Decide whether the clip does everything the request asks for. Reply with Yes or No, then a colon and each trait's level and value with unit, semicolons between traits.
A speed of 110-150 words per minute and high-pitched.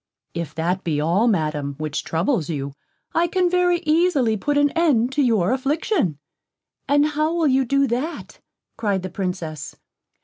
No: average, 160 wpm; high, 240 Hz